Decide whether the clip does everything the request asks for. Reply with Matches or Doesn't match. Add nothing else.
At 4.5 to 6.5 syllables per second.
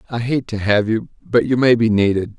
Matches